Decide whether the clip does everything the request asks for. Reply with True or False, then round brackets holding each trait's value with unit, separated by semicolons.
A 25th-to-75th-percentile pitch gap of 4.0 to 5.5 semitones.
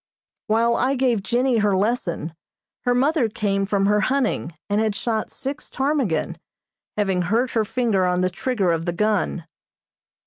True (4.3 semitones)